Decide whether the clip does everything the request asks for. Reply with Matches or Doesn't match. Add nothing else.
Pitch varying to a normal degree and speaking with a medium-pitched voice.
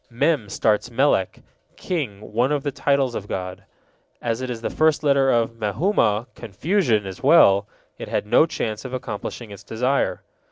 Doesn't match